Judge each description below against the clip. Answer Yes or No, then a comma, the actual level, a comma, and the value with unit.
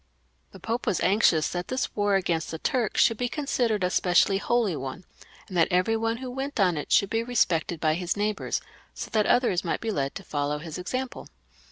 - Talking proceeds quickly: Yes, fast, 210 wpm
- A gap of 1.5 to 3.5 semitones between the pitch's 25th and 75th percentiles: No, average, 5.1 semitones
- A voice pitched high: Yes, high, 195 Hz